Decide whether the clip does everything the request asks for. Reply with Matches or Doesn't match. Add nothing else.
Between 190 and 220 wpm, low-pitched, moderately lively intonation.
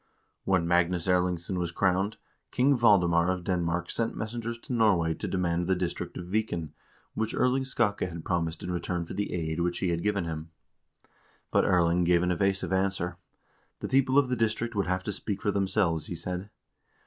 Matches